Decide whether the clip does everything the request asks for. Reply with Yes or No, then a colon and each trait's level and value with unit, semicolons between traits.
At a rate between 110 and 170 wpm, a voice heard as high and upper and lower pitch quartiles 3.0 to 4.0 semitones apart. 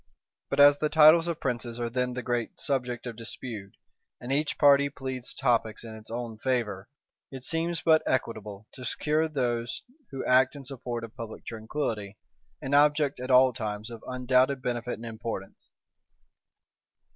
No: average, 160 wpm; low, 125 Hz; average, 3.3 semitones